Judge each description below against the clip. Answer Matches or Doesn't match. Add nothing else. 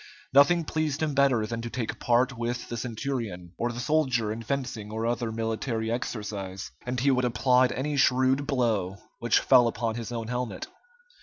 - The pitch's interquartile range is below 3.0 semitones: Matches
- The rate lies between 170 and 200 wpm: Matches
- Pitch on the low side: Matches